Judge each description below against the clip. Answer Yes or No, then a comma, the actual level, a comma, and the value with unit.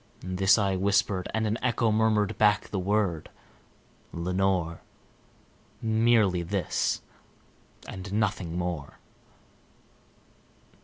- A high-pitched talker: No, low, 100 Hz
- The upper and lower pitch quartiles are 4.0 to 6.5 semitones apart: No, average, 2.9 semitones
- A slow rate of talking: Yes, slow, 90 wpm